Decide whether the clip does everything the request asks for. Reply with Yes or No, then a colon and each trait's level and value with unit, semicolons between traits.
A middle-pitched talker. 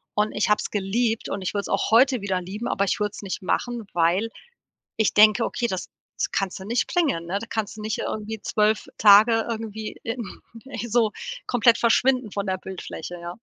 No: high, 215 Hz